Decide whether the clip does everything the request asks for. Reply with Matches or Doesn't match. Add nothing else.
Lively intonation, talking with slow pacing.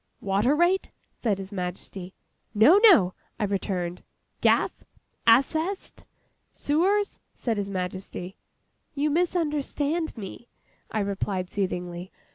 Matches